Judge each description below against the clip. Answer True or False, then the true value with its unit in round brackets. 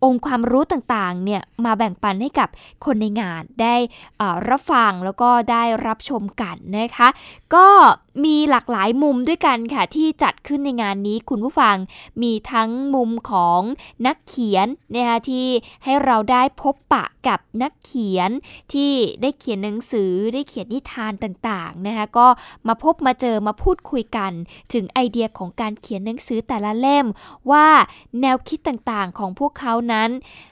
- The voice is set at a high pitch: True (240 Hz)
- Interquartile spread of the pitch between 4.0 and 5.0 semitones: False (3.6 semitones)